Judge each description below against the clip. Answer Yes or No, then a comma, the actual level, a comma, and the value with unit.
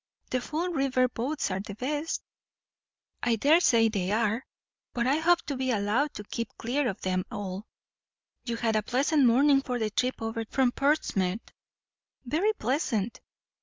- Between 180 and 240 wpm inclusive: No, average, 160 wpm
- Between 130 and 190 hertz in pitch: No, high, 245 Hz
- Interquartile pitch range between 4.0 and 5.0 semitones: Yes, average, 4.7 semitones